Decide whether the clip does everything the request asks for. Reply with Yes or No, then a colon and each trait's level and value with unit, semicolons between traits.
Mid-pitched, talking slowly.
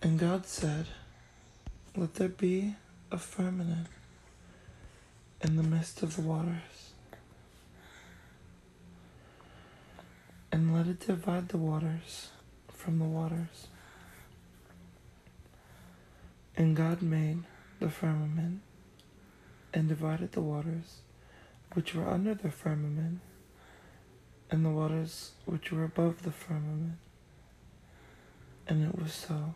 Yes: medium, 160 Hz; slow, 100 wpm